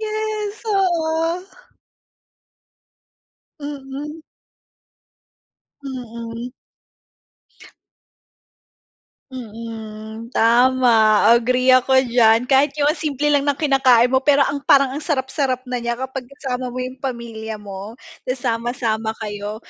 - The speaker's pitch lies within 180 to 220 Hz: No, very high, 255 Hz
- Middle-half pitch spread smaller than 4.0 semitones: Yes, average, 3.5 semitones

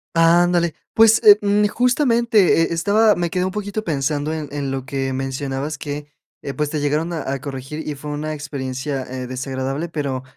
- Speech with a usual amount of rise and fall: Yes, average, 4.4 semitones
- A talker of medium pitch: Yes, medium, 150 Hz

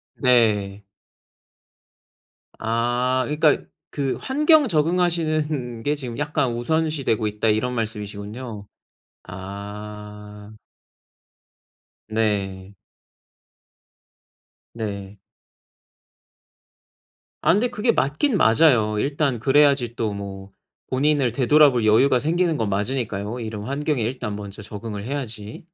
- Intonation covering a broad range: Yes, wide, 5.7 semitones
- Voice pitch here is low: Yes, low, 120 Hz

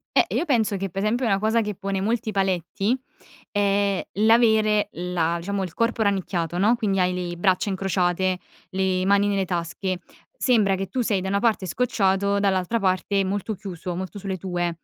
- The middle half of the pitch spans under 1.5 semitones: No, narrow, 2.4 semitones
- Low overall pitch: No, high, 195 Hz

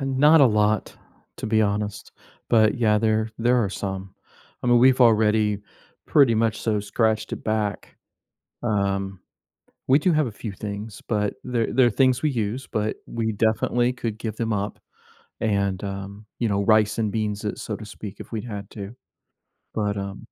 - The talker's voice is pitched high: No, low, 110 Hz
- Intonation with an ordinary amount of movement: No, narrow, 2.3 semitones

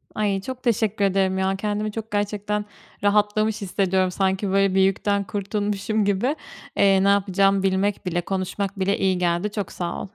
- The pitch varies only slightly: Yes, narrow, 1.5 semitones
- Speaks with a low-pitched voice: No, high, 200 Hz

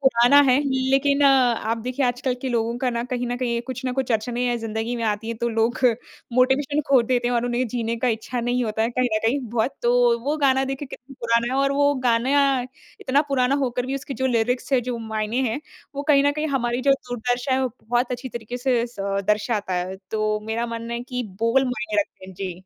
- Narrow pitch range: Yes, narrow, 2.3 semitones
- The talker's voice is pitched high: Yes, high, 245 Hz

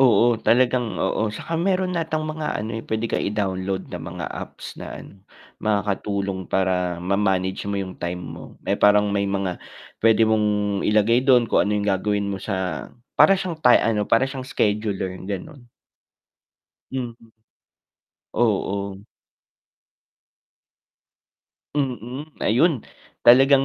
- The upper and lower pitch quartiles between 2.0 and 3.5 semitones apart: No, average, 4.3 semitones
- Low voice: Yes, low, 105 Hz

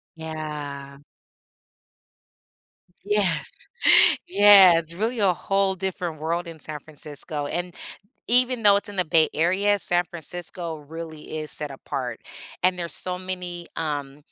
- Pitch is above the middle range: No, medium, 170 Hz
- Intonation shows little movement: No, average, 3.6 semitones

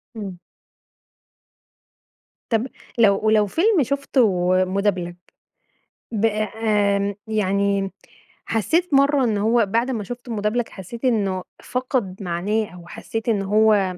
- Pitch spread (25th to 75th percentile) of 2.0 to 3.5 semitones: Yes, average, 3.0 semitones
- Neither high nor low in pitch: No, high, 215 Hz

